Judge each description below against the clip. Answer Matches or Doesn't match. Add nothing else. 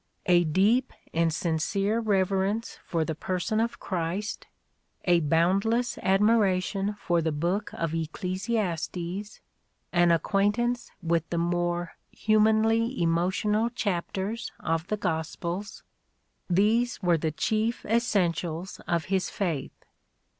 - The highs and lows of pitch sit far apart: Doesn't match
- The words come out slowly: Matches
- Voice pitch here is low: Doesn't match